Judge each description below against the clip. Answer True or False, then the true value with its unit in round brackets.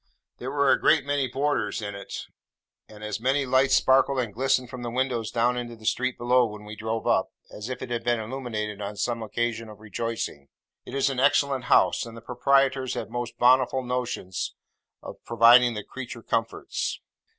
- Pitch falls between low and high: False (120 Hz)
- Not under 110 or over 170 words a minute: False (190 wpm)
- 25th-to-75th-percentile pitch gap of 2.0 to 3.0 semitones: True (2.7 semitones)